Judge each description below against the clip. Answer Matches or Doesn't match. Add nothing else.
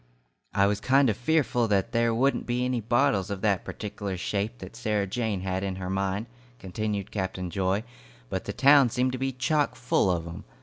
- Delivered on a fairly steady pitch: Doesn't match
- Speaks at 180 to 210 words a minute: Matches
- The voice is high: Doesn't match